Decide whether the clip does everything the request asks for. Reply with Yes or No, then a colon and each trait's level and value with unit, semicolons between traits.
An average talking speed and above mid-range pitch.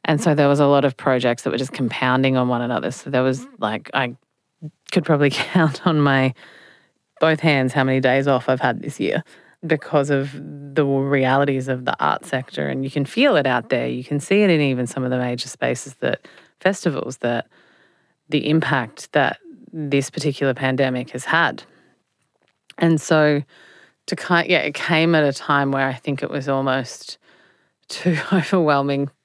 No: average, 185 wpm; medium, 140 Hz